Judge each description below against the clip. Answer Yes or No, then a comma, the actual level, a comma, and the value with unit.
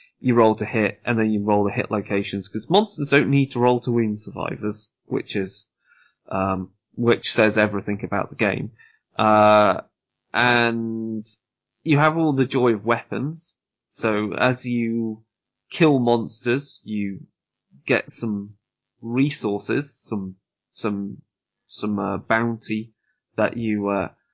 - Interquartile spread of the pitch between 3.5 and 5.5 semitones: No, average, 2.9 semitones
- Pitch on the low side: Yes, low, 110 Hz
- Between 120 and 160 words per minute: Yes, slow, 135 wpm